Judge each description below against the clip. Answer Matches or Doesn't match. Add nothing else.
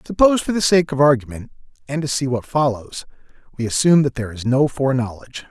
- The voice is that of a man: Matches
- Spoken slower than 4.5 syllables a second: Doesn't match